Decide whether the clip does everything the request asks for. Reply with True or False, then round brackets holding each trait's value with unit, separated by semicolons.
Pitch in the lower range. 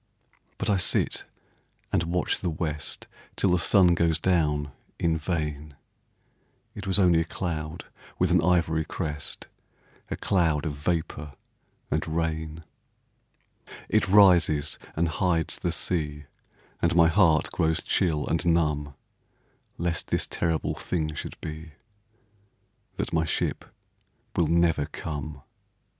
True (80 Hz)